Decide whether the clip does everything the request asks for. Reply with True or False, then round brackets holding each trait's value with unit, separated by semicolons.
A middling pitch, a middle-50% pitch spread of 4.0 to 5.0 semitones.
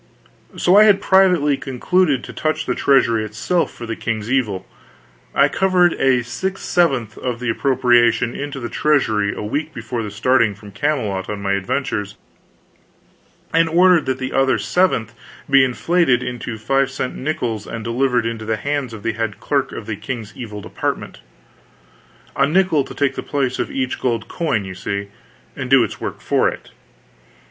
False (125 Hz; 4.7 semitones)